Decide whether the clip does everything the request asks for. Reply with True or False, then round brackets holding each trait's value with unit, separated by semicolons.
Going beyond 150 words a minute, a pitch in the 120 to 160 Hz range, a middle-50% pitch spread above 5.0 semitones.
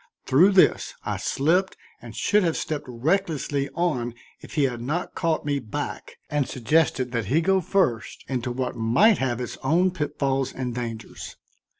True (165 wpm; 140 Hz; 5.4 semitones)